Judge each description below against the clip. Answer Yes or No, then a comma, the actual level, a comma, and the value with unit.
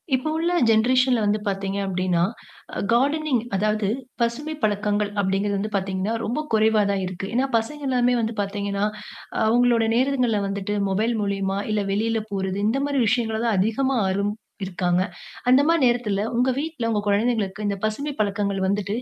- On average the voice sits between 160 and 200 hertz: No, high, 215 Hz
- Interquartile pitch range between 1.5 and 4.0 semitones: Yes, average, 3.7 semitones